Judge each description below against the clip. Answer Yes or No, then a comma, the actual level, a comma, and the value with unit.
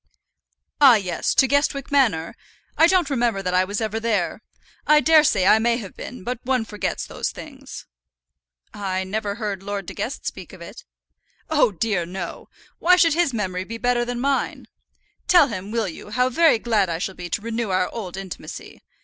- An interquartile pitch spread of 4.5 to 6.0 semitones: Yes, average, 5.1 semitones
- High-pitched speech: Yes, high, 225 Hz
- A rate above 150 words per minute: Yes, average, 185 wpm